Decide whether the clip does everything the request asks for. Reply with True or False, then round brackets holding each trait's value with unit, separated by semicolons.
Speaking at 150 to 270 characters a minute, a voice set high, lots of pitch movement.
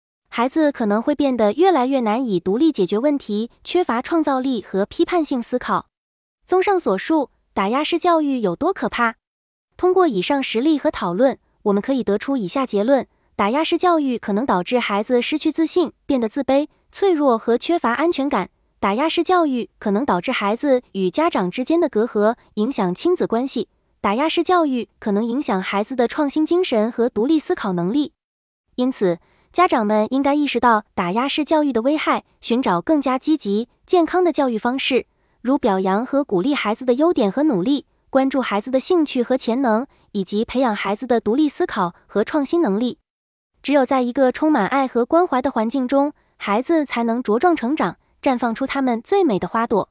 False (290 characters per minute; 260 Hz; 5.8 semitones)